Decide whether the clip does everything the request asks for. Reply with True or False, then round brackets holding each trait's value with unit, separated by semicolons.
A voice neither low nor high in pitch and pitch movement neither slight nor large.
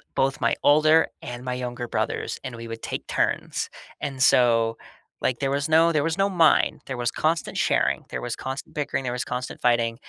False (130 Hz; 4.1 semitones)